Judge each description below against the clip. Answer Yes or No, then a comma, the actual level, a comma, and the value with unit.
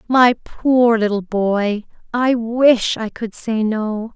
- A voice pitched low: No, high, 225 Hz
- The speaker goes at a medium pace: Yes, average, 145 wpm